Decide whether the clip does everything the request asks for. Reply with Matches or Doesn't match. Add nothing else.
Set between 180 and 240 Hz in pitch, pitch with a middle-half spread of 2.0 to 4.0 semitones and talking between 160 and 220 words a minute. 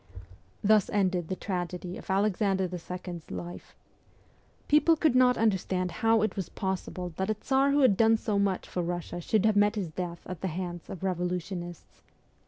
Matches